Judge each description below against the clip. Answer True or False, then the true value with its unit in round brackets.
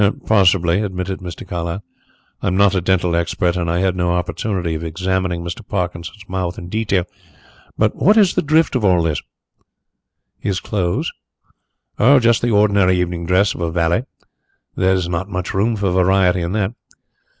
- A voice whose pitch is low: True (95 Hz)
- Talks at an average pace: True (170 wpm)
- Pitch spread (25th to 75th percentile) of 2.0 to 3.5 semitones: True (2.7 semitones)